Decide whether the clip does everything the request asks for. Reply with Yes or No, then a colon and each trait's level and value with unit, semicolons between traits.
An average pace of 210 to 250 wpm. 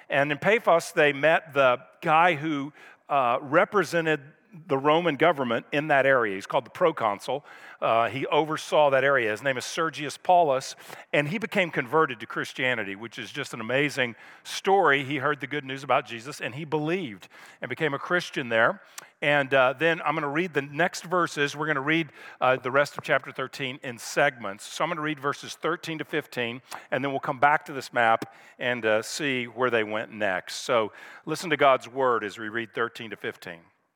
No: average, 200 wpm